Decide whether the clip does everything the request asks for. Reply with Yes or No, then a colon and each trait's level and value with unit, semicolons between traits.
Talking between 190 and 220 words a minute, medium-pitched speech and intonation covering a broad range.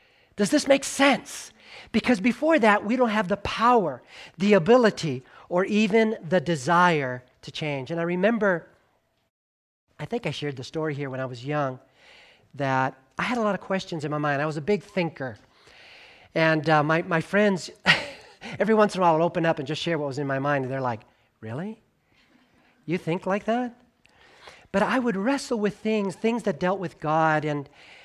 Yes: average, 195 wpm; medium, 175 Hz; wide, 6.2 semitones